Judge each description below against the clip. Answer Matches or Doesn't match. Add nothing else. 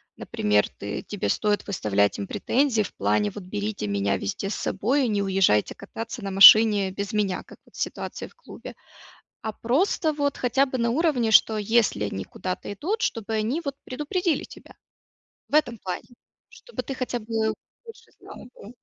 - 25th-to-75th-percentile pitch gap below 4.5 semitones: Doesn't match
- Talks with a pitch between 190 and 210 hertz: Doesn't match